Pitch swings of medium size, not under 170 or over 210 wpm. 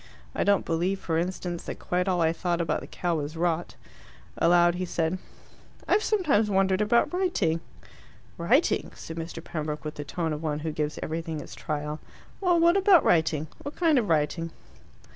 Yes: average, 3.5 semitones; average, 180 wpm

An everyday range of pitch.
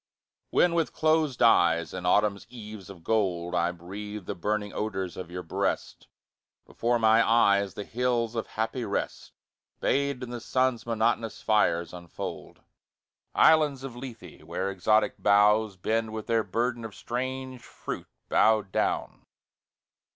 Yes: average, 3.7 semitones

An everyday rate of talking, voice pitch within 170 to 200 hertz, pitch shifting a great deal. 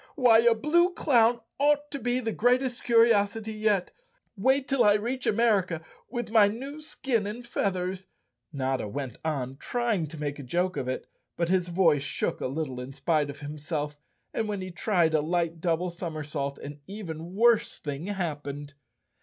Yes: average, 180 wpm; medium, 185 Hz; wide, 7.4 semitones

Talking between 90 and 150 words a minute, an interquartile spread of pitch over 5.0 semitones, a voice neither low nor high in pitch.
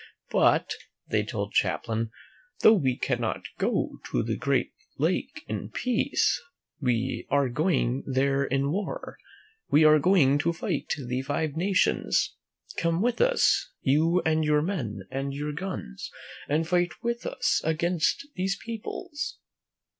Yes: average, 140 wpm; wide, 5.4 semitones; medium, 150 Hz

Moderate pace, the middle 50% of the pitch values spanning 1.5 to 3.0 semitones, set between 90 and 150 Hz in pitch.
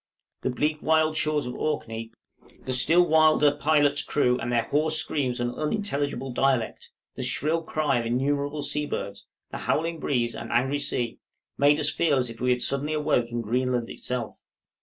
No: average, 175 wpm; average, 3.7 semitones; medium, 140 Hz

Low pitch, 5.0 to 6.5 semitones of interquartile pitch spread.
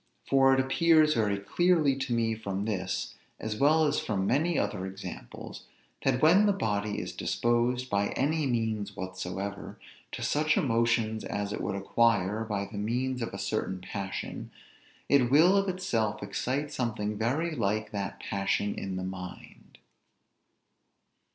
Yes: low, 115 Hz; average, 5.3 semitones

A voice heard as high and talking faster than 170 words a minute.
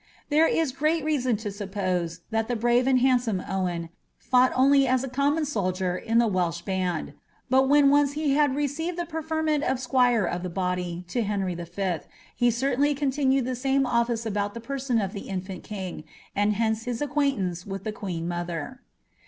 Yes: high, 235 Hz; average, 185 wpm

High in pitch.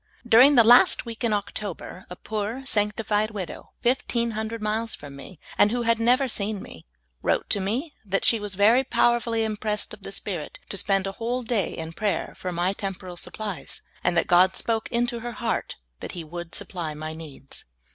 Yes: high, 210 Hz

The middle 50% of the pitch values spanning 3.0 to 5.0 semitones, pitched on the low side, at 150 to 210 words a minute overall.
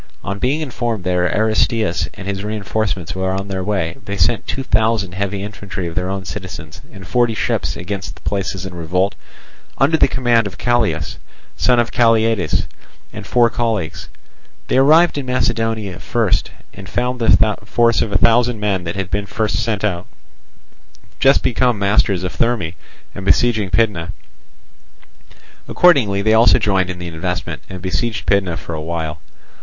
Yes: average, 3.9 semitones; low, 100 Hz; average, 165 wpm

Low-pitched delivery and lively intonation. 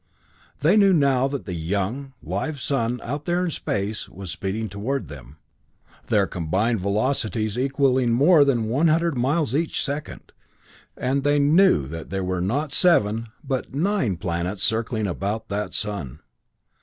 Yes: low, 120 Hz; wide, 6.1 semitones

